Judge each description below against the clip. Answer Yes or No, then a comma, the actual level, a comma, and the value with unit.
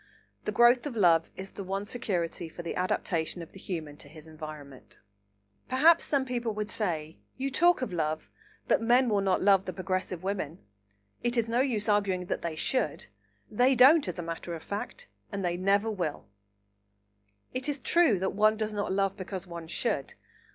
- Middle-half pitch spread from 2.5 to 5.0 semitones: No, wide, 5.5 semitones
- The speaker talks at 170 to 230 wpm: Yes, average, 185 wpm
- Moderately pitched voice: No, high, 195 Hz